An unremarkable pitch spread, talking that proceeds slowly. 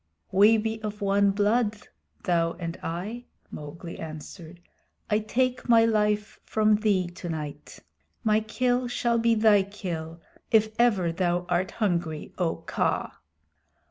Yes: average, 4.2 semitones; slow, 125 wpm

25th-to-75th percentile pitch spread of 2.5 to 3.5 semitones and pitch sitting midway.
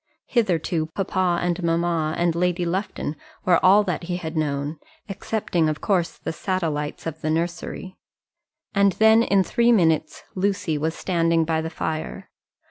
Yes: average, 2.8 semitones; medium, 170 Hz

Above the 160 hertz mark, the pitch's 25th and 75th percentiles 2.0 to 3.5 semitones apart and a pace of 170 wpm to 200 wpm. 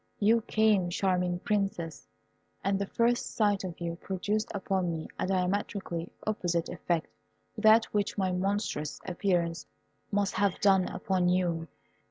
No: high, 190 Hz; narrow, 2.6 semitones; average, 140 wpm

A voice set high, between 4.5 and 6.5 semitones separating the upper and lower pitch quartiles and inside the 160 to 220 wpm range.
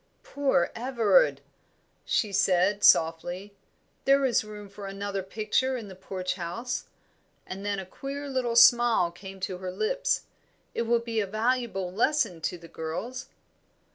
No: high, 205 Hz; average, 4.8 semitones; average, 145 wpm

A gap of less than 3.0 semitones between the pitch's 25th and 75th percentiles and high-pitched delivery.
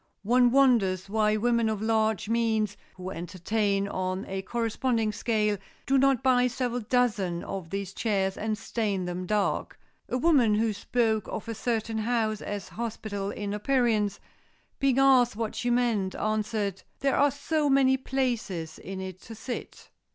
No: average, 3.5 semitones; high, 220 Hz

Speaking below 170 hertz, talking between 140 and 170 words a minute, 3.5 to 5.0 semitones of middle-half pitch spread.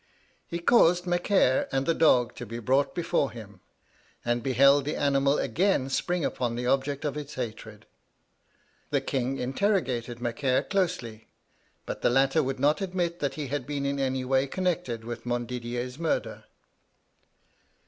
Yes: low, 135 Hz; average, 150 wpm; average, 4.1 semitones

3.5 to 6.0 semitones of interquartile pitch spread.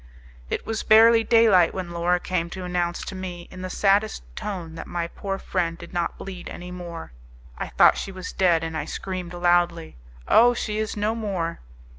No: average, 2.7 semitones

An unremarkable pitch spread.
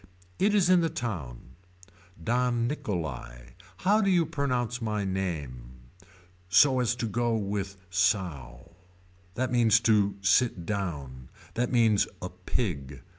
No: wide, 6.9 semitones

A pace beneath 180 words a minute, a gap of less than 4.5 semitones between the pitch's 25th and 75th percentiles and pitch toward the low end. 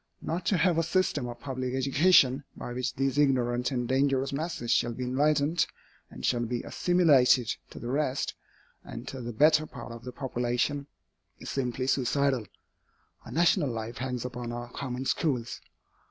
Yes: average, 165 wpm; average, 3.0 semitones; low, 130 Hz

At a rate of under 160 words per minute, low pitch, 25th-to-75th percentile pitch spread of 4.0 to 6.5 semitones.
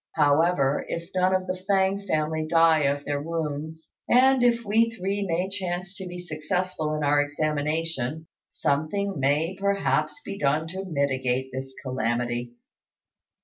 No: average, 145 wpm; medium, 160 Hz; average, 4.6 semitones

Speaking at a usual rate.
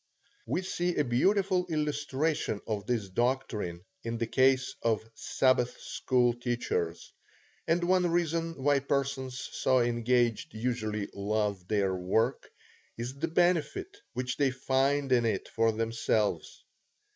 No: slow, 125 wpm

